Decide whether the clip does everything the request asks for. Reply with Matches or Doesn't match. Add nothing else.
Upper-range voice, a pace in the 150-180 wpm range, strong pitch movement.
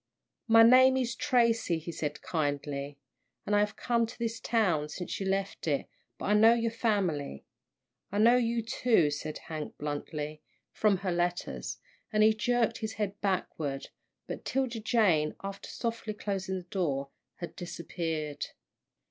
Matches